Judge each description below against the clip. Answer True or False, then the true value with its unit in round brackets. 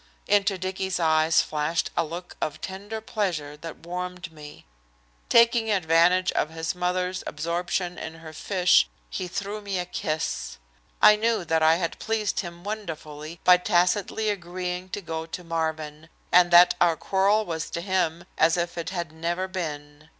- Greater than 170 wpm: False (160 wpm)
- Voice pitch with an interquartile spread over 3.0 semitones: False (2.7 semitones)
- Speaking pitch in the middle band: True (175 Hz)